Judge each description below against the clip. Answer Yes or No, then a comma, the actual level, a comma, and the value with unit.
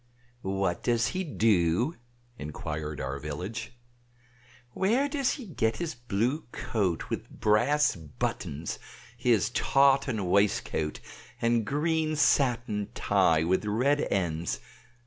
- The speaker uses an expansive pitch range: Yes, wide, 8.0 semitones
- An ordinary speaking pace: No, slow, 110 wpm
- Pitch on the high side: No, low, 110 Hz